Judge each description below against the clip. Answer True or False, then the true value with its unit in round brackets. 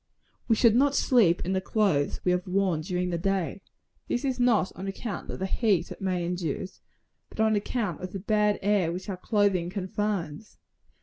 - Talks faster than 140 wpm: True (190 wpm)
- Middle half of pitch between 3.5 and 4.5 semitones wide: False (3.0 semitones)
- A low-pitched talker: False (195 Hz)